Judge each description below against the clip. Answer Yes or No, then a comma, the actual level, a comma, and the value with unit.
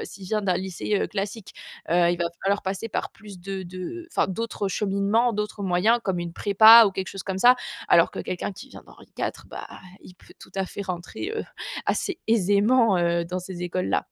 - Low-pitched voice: No, high, 195 Hz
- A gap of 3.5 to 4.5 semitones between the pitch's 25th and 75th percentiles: No, average, 2.9 semitones